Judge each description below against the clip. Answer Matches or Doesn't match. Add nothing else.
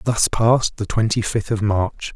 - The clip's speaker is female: Doesn't match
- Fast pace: Doesn't match